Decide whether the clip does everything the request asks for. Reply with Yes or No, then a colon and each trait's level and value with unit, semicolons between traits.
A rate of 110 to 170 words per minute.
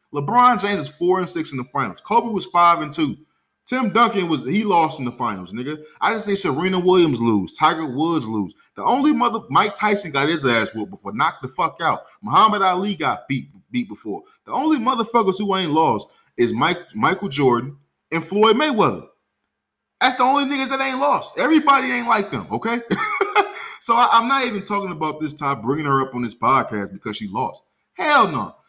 No: average, 200 wpm